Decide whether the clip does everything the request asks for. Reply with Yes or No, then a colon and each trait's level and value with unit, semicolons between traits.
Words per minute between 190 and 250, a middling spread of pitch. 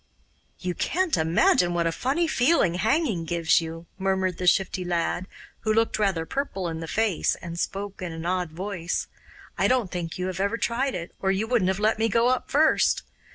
Yes: average, 200 wpm; average, 4.7 semitones